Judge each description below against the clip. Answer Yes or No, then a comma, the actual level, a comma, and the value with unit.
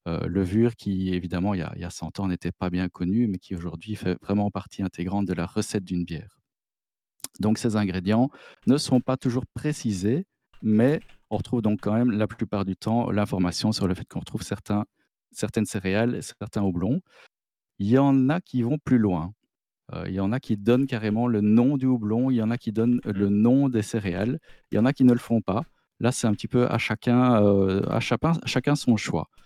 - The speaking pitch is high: No, low, 110 Hz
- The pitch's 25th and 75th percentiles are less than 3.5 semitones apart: No, average, 3.8 semitones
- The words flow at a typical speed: No, fast, 225 wpm